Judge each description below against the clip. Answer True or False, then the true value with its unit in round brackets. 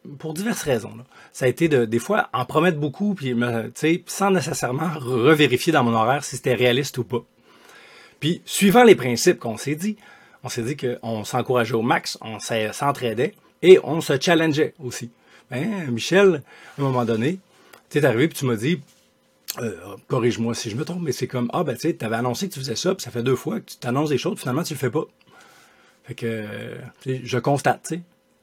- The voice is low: True (130 Hz)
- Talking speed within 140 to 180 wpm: False (215 wpm)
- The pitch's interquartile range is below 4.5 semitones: False (5.5 semitones)